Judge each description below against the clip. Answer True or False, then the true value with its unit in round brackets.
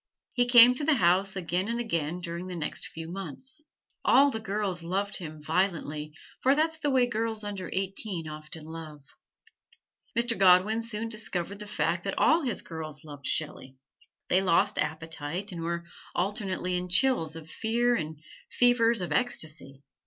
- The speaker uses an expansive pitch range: True (5.8 semitones)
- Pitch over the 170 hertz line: True (185 Hz)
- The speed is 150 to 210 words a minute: True (160 wpm)